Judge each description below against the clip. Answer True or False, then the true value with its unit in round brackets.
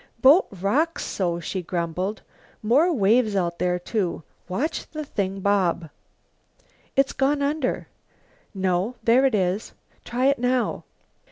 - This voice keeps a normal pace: False (125 wpm)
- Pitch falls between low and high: False (210 Hz)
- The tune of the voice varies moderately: False (6.6 semitones)